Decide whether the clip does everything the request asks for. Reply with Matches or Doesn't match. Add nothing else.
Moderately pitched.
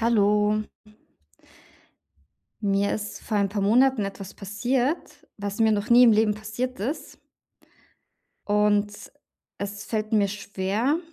Doesn't match